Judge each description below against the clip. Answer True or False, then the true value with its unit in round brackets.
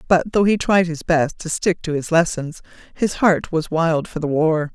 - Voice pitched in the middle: True (165 Hz)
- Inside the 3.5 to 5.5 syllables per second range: True (4.5 syllables/s)